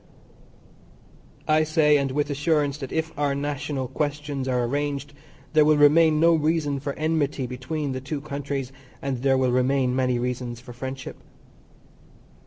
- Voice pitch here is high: No, medium, 140 Hz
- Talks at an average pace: Yes, average, 150 wpm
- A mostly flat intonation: Yes, narrow, 2.3 semitones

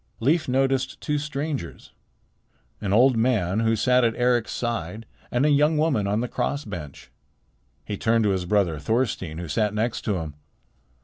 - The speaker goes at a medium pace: Yes, average, 170 wpm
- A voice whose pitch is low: Yes, low, 115 Hz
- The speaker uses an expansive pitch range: No, average, 4.8 semitones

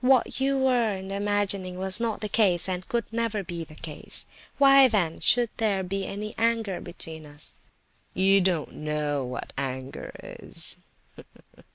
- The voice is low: No, high, 195 Hz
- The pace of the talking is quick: No, average, 150 wpm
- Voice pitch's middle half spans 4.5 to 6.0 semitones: Yes, average, 5.0 semitones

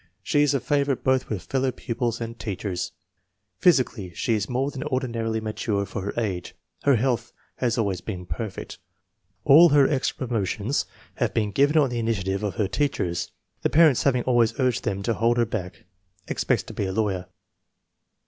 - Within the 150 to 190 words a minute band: Yes, average, 180 wpm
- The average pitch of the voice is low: Yes, low, 115 Hz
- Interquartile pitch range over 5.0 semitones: No, average, 4.4 semitones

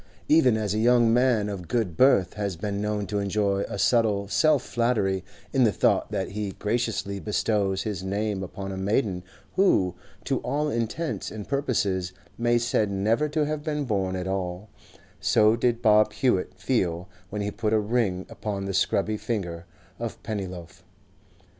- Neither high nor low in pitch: No, low, 105 Hz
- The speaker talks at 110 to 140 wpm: No, average, 170 wpm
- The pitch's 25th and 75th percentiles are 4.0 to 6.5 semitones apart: No, average, 3.4 semitones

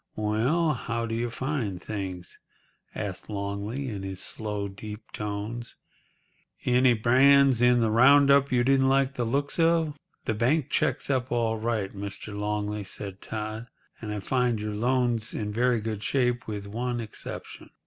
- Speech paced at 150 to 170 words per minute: Yes, average, 155 wpm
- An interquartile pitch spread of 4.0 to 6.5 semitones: No, average, 3.4 semitones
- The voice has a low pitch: Yes, low, 115 Hz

